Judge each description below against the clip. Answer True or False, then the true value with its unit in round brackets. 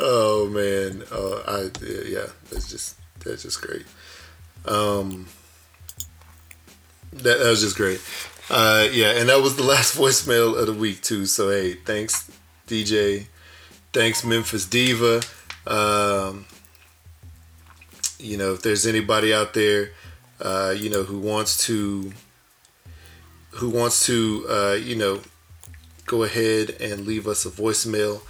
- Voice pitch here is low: True (100 Hz)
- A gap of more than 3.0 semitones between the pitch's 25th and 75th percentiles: True (4.1 semitones)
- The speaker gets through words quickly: False (135 wpm)